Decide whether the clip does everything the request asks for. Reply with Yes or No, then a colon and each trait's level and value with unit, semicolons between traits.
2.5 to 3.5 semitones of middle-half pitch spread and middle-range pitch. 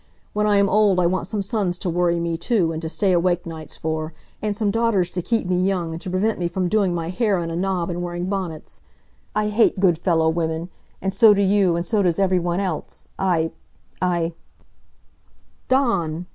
Yes: average, 2.8 semitones; medium, 180 Hz